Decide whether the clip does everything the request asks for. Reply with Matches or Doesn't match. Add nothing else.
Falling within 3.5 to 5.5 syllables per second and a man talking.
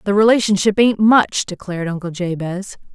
Doesn't match